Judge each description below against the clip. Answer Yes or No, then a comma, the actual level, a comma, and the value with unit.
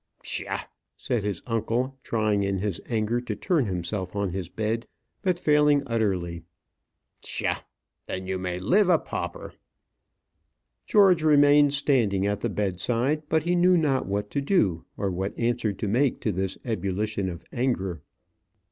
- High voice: No, low, 110 Hz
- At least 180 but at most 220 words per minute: No, average, 150 wpm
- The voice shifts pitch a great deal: Yes, wide, 6.7 semitones